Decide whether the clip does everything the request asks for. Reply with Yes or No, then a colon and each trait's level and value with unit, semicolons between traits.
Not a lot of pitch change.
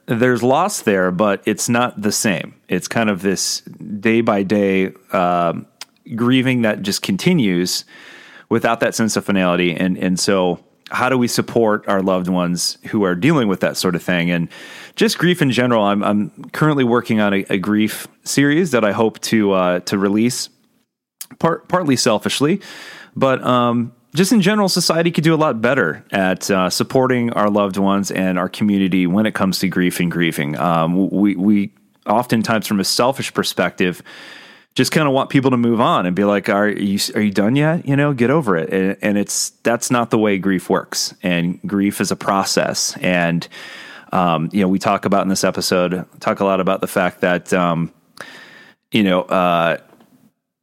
No: average, 4.5 semitones